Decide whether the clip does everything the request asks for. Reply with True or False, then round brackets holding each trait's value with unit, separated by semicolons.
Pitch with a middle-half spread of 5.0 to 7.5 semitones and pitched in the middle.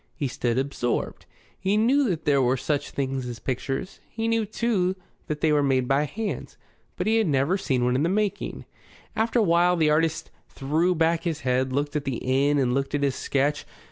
True (5.3 semitones; 150 Hz)